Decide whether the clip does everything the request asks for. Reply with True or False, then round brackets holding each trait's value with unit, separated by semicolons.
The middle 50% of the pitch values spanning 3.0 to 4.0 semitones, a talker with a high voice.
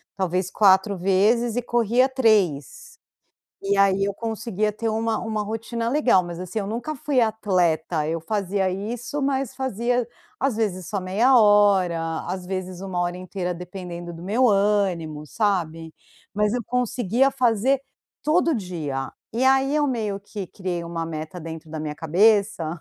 False (4.6 semitones; 200 Hz)